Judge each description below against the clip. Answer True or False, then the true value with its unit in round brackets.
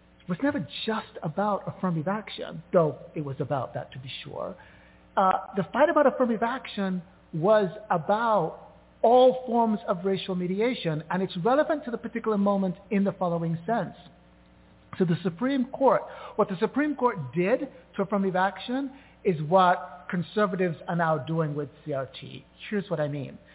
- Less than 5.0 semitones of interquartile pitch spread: False (5.4 semitones)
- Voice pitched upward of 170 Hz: True (190 Hz)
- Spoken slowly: False (160 wpm)